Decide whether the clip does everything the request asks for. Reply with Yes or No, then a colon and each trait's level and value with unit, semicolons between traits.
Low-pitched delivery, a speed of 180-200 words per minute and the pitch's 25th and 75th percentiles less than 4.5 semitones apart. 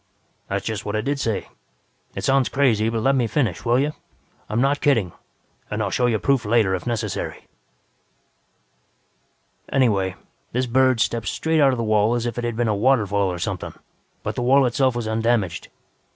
Yes: low, 115 Hz; average, 185 wpm; average, 3.4 semitones